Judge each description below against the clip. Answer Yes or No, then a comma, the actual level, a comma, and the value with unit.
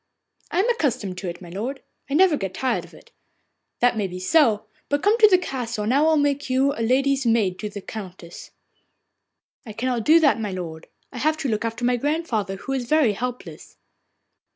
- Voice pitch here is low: No, high, 245 Hz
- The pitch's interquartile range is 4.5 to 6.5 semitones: Yes, wide, 5.6 semitones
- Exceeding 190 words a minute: Yes, fast, 205 wpm